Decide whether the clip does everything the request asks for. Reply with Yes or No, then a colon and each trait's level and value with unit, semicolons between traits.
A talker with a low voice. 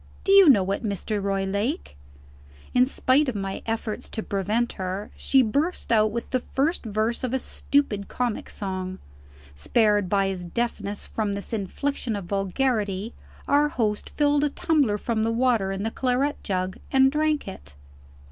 No: high, 220 Hz